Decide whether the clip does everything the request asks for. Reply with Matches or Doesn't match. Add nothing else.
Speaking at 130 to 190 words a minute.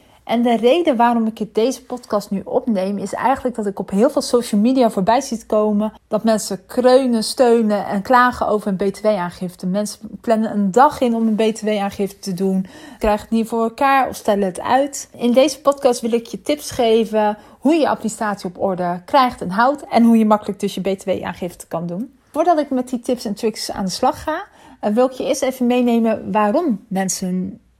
Doesn't match